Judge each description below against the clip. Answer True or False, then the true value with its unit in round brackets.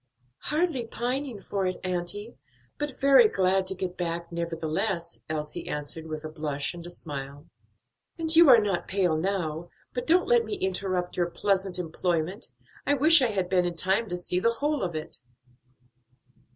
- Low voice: False (185 Hz)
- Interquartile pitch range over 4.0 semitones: True (5.4 semitones)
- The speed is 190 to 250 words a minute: False (170 wpm)